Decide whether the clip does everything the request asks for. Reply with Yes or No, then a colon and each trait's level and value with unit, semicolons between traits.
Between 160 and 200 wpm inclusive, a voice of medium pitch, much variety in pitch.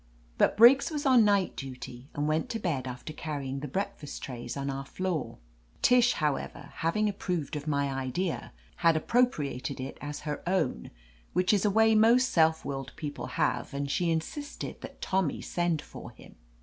Yes: average, 180 wpm; medium, 160 Hz; wide, 6.4 semitones